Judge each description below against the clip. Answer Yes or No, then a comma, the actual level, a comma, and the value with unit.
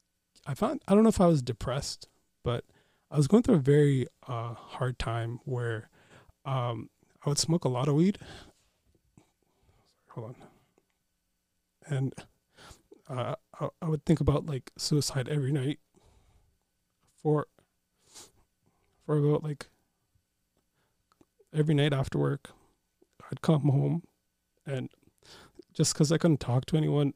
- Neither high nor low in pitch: Yes, medium, 145 Hz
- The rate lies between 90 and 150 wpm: Yes, slow, 135 wpm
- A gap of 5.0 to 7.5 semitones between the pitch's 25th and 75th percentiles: No, average, 4.3 semitones